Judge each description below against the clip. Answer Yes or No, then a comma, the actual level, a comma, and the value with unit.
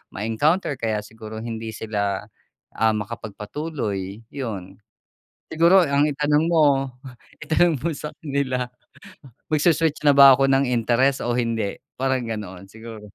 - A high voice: No, low, 125 Hz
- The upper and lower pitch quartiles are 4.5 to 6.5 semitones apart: Yes, average, 4.8 semitones